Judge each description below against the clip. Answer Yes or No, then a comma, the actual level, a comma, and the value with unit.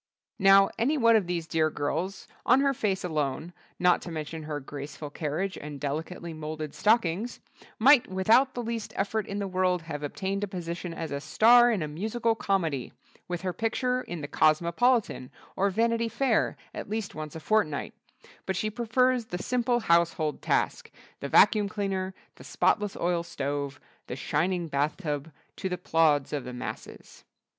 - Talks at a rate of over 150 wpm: Yes, average, 160 wpm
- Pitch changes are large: Yes, wide, 5.9 semitones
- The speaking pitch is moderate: Yes, medium, 180 Hz